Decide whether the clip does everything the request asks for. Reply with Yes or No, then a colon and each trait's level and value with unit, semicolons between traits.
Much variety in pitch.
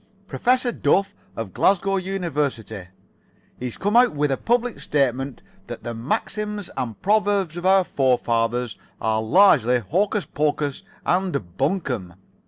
Yes: wide, 8.2 semitones